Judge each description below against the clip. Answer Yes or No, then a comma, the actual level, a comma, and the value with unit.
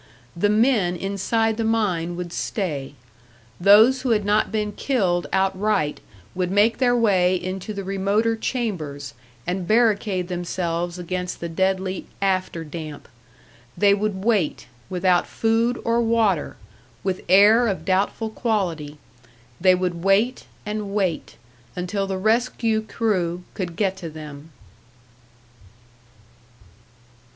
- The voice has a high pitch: Yes, high, 195 Hz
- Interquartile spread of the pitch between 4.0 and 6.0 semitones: No, average, 3.6 semitones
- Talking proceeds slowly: Yes, slow, 120 wpm